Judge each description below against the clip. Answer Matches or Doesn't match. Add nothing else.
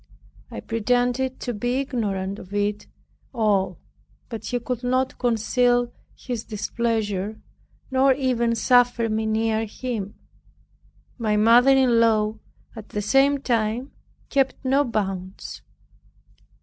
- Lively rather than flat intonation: Doesn't match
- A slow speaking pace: Matches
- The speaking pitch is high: Matches